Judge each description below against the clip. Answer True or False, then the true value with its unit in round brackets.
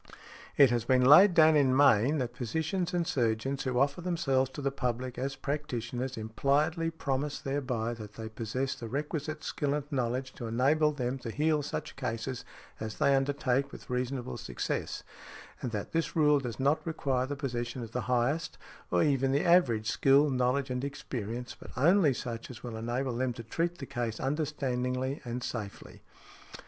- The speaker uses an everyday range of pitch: True (3.1 semitones)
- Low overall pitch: True (130 Hz)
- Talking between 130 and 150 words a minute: False (175 wpm)